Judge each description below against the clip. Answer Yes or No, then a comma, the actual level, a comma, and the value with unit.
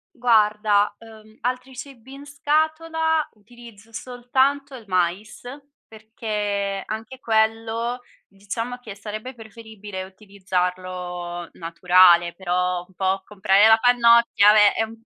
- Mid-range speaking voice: No, high, 215 Hz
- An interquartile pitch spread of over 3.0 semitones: Yes, average, 3.9 semitones